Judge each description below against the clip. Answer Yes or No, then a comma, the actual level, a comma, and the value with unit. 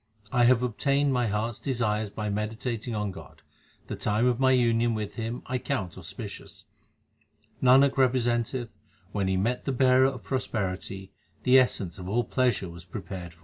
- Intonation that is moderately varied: Yes, average, 4.1 semitones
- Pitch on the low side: Yes, low, 115 Hz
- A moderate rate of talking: Yes, average, 180 wpm